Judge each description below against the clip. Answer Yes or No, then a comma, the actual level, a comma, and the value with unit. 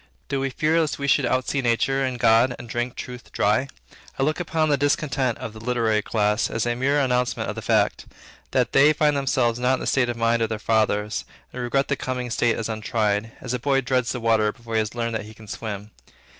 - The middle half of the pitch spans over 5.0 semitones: No, average, 3.2 semitones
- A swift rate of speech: Yes, fast, 235 wpm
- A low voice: Yes, low, 120 Hz